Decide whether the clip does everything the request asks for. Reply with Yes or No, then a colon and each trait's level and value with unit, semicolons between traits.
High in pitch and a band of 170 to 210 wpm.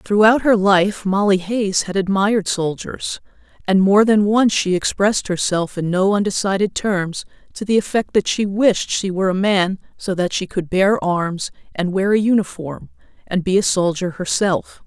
Yes: high, 195 Hz; average, 180 wpm